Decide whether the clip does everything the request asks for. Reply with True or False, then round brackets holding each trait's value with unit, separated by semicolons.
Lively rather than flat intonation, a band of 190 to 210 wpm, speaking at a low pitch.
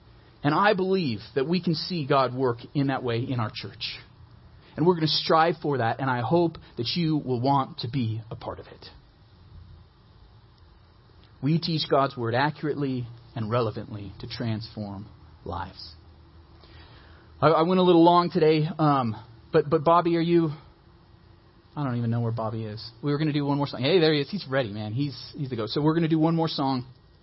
True (6.1 semitones; 205 wpm; 125 Hz)